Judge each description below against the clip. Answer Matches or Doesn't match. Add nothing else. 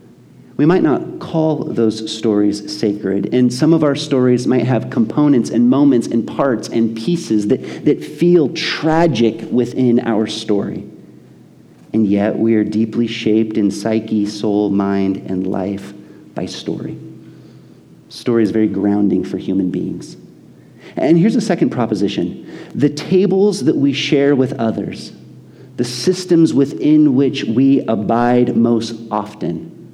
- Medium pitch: Doesn't match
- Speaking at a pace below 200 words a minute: Matches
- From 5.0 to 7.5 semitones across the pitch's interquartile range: Matches